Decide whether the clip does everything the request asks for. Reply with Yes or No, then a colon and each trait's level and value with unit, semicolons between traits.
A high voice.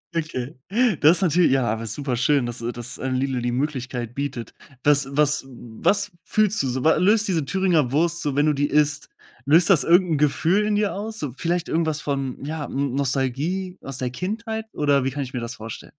No: medium, 145 Hz